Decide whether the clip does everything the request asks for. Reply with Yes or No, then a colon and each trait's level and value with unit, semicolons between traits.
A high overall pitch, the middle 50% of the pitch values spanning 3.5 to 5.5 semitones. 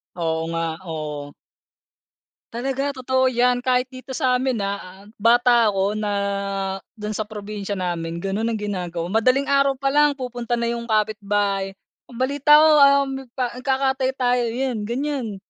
Yes: high, 235 Hz; average, 4.4 semitones